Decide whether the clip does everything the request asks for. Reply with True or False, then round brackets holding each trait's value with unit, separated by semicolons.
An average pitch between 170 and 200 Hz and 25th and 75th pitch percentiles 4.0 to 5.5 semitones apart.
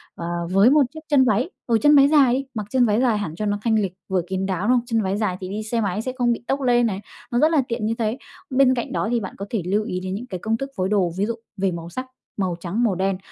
False (215 Hz; 4.3 semitones)